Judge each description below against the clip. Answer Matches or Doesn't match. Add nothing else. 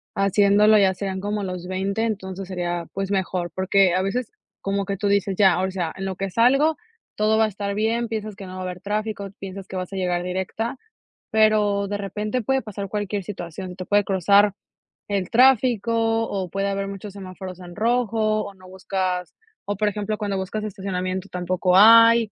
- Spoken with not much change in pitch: Matches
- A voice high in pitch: Matches